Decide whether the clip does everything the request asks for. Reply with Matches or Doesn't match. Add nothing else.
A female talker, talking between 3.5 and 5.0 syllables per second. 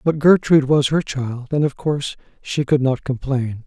Doesn't match